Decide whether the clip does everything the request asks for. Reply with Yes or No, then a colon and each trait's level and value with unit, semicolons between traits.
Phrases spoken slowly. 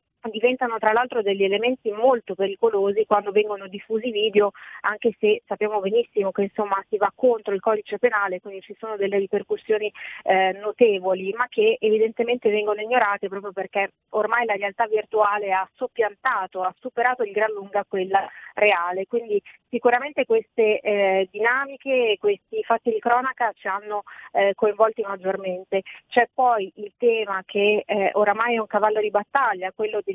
No: average, 155 wpm